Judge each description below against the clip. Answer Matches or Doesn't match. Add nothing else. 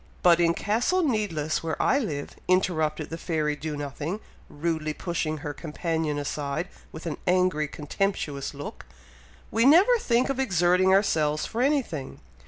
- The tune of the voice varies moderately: Matches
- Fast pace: Doesn't match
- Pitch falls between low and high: Matches